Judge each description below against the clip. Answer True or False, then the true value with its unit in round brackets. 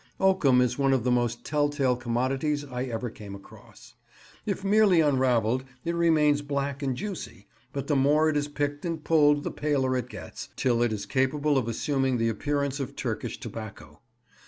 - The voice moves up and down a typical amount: True (3.1 semitones)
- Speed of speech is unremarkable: True (180 wpm)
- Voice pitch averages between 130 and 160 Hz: True (135 Hz)